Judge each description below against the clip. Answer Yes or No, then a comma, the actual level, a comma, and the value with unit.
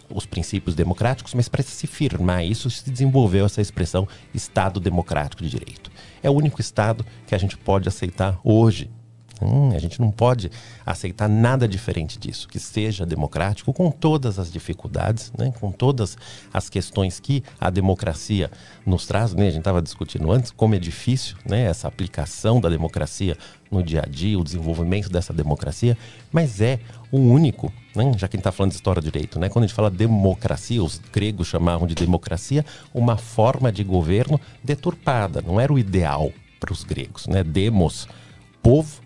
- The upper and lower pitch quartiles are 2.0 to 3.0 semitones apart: No, average, 4.7 semitones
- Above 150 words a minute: Yes, average, 175 wpm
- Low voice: Yes, low, 105 Hz